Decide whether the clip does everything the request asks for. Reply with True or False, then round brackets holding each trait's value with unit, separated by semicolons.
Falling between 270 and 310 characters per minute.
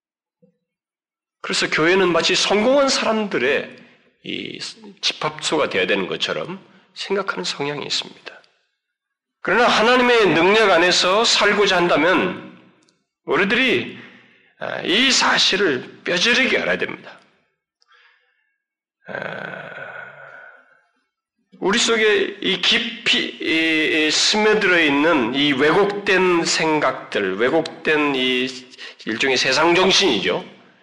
False (210 characters per minute)